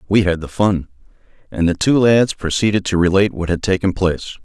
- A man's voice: Yes, male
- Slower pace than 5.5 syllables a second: No, 5.9 syllables/s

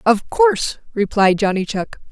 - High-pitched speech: Yes, high, 225 Hz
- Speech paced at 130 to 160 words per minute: Yes, average, 140 wpm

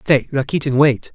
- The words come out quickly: No, average, 155 wpm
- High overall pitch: No, low, 135 Hz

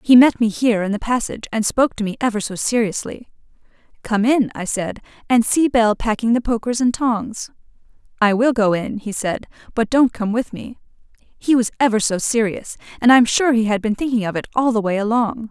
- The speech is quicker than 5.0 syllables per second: Yes, 5.5 syllables/s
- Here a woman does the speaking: Yes, female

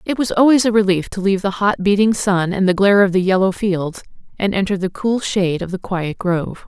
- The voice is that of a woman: Yes, female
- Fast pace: Yes, fast, 245 wpm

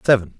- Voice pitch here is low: Yes, low, 110 Hz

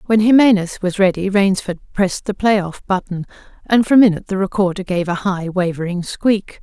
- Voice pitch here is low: No, high, 195 Hz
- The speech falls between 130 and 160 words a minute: No, average, 180 wpm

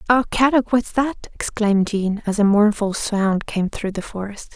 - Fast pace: No, average, 185 wpm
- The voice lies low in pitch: No, high, 215 Hz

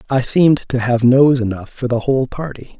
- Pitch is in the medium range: No, low, 130 Hz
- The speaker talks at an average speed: No, fast, 215 wpm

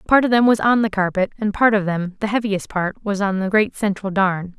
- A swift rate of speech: Yes, fast, 235 wpm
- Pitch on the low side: No, high, 205 Hz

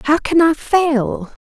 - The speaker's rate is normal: Yes, average, 170 wpm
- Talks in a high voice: Yes, very high, 300 Hz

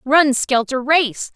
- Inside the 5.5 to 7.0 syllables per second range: No, 3.2 syllables/s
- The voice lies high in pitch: Yes, very high, 270 Hz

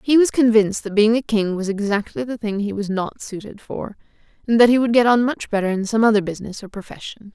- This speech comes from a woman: Yes, female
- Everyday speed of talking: No, fast, 245 wpm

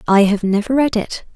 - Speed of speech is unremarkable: No, fast, 220 wpm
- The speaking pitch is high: Yes, high, 215 Hz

